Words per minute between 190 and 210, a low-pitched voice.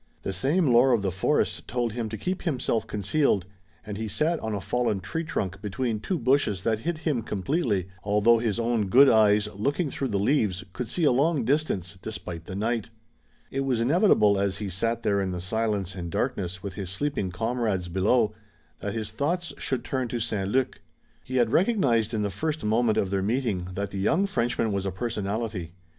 Yes: average, 200 wpm; low, 110 Hz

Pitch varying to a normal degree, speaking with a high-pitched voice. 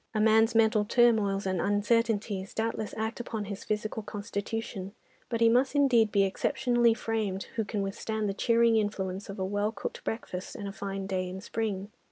No: narrow, 2.3 semitones; high, 215 Hz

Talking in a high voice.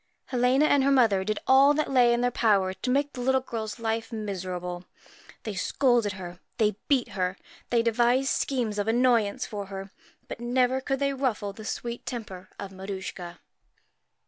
Yes: high, 230 Hz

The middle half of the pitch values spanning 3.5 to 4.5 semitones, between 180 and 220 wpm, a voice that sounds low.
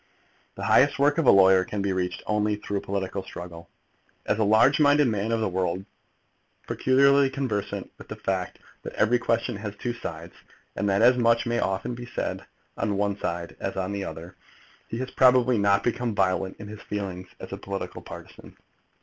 Yes: average, 4.1 semitones; average, 190 wpm; low, 105 Hz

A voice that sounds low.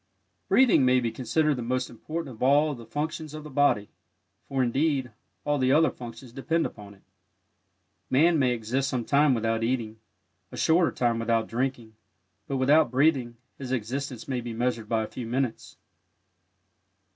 Yes: low, 130 Hz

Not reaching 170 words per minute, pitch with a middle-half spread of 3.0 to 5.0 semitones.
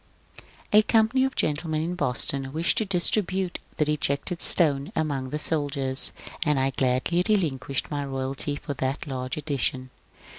Yes: average, 160 wpm; average, 4.4 semitones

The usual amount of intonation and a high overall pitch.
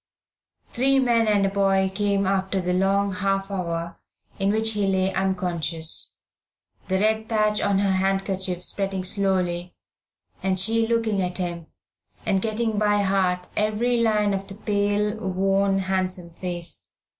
No: narrow, 2.0 semitones; high, 195 Hz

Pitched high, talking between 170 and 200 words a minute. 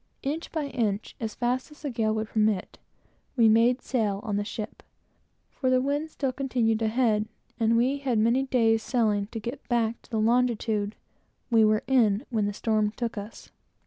Yes: high, 230 Hz; average, 185 wpm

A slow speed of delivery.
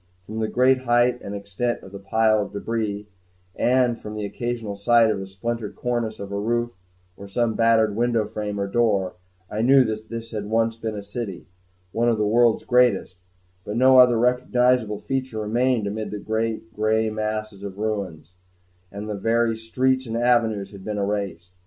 No: average, 185 wpm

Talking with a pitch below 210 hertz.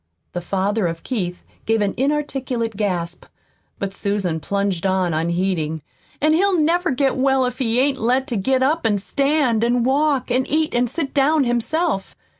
No: high, 240 Hz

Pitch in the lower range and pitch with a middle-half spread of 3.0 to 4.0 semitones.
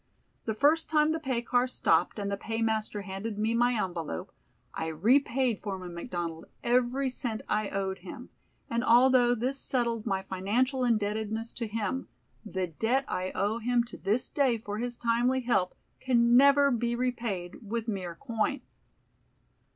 No: high, 230 Hz; average, 3.7 semitones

